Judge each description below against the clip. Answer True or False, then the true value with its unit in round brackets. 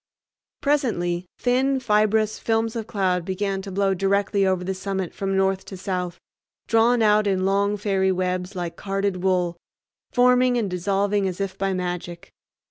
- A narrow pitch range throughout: True (2.3 semitones)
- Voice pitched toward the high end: True (195 Hz)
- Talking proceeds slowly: False (155 wpm)